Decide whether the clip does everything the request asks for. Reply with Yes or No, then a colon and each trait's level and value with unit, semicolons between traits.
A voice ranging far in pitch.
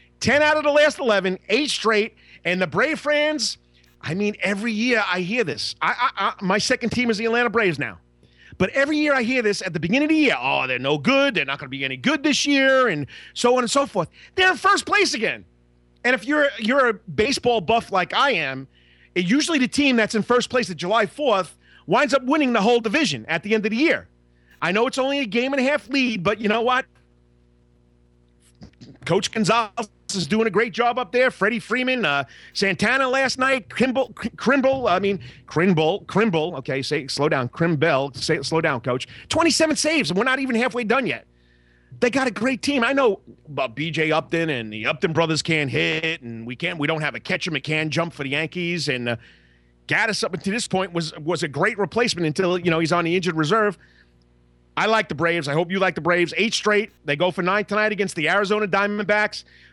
Yes: wide, 7.8 semitones